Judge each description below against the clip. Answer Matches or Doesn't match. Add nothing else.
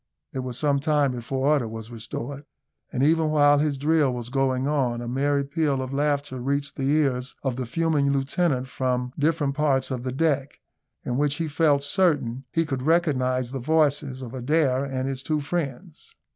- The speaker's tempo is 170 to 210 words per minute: Matches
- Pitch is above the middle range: Doesn't match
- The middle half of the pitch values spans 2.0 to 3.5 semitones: Matches